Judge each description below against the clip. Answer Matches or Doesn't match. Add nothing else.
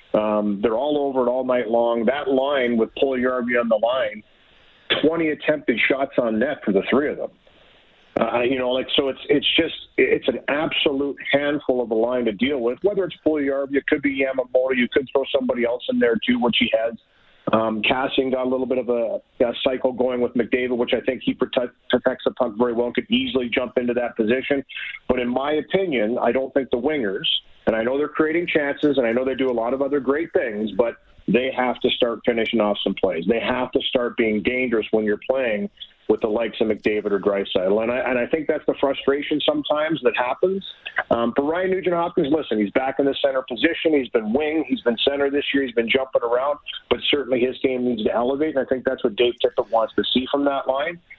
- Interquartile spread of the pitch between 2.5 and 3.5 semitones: Matches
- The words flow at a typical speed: Doesn't match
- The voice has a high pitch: Doesn't match